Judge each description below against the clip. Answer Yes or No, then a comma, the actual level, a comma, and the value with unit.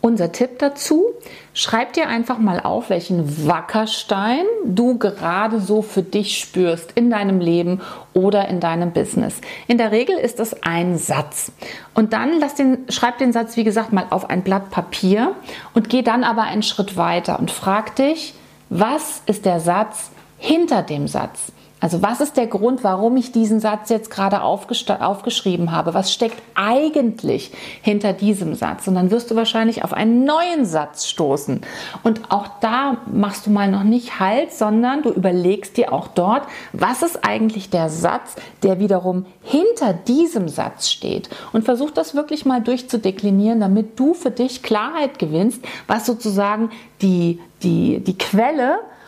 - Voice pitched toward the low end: No, high, 220 Hz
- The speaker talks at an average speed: Yes, average, 165 wpm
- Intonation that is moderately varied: Yes, average, 4.4 semitones